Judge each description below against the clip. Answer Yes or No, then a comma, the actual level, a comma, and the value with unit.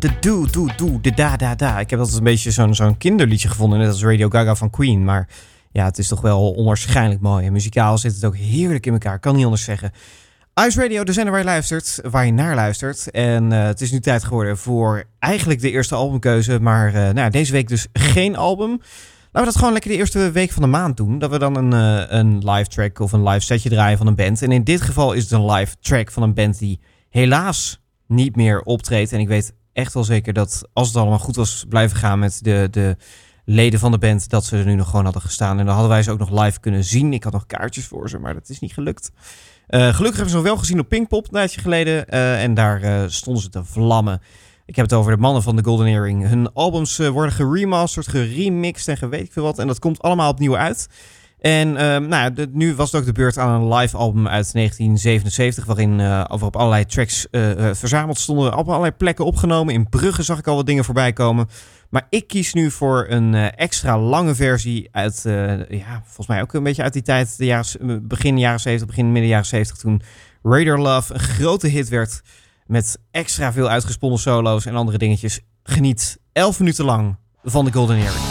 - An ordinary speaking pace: No, fast, 235 wpm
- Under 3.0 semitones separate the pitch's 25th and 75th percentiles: No, average, 4.6 semitones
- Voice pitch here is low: Yes, low, 115 Hz